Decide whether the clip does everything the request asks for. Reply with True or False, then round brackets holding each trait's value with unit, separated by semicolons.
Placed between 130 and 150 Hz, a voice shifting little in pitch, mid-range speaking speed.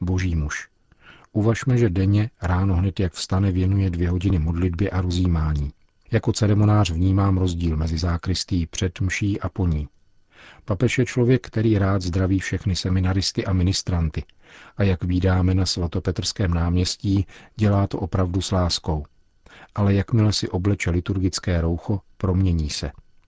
False (95 Hz; 2.1 semitones; 140 wpm)